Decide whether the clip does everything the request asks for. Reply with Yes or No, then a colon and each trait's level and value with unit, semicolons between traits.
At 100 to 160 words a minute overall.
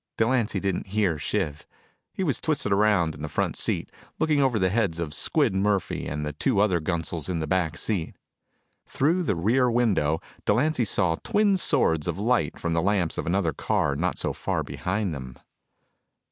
No: average, 180 wpm